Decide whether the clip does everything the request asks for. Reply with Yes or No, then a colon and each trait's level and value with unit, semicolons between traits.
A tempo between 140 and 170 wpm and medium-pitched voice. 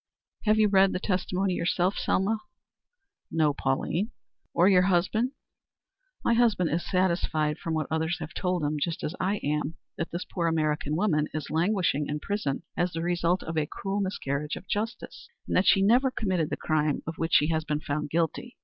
No: average, 185 wpm; medium, 170 Hz